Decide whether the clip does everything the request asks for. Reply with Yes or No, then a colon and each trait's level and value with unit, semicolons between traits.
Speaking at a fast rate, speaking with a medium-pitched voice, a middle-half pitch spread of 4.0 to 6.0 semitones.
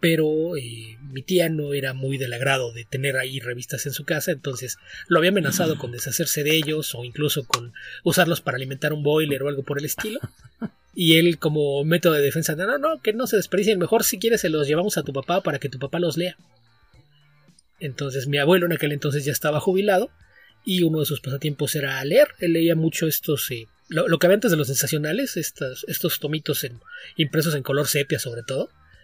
No: fast, 215 wpm; medium, 150 Hz; average, 3.6 semitones